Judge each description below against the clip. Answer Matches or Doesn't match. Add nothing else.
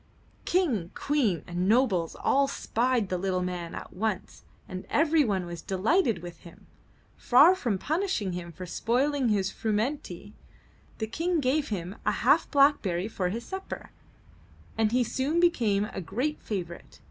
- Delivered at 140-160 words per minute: Matches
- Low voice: Doesn't match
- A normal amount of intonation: Doesn't match